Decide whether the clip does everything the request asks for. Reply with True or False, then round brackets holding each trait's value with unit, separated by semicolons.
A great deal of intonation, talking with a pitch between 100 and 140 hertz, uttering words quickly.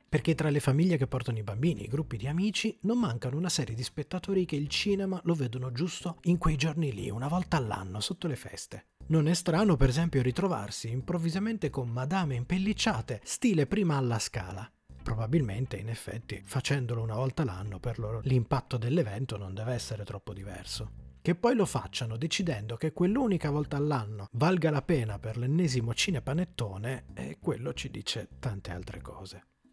True (6.7 semitones; 135 Hz; 175 wpm)